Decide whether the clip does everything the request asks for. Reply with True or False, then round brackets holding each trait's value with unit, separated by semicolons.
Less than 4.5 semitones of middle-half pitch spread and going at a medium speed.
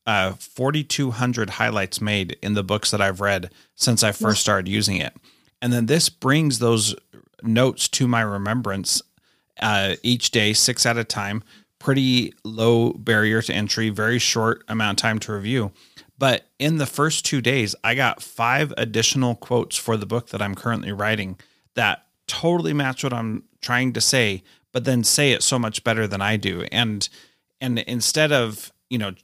True (3.5 semitones; 175 wpm)